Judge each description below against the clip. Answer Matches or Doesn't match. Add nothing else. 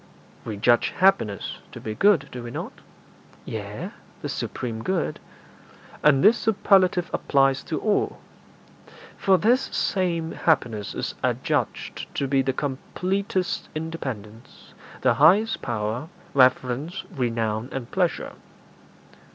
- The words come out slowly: Matches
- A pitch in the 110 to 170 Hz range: Matches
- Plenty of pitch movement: Matches